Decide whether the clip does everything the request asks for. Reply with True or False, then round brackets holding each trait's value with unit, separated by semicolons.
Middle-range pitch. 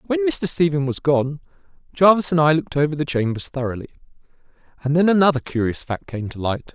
True (155 Hz)